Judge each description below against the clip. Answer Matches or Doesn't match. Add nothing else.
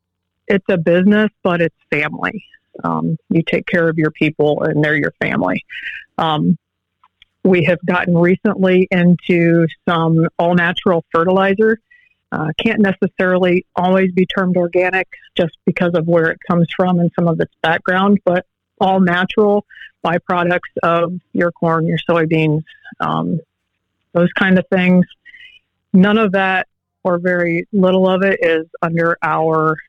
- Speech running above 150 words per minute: Doesn't match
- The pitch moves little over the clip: Matches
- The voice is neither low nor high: Matches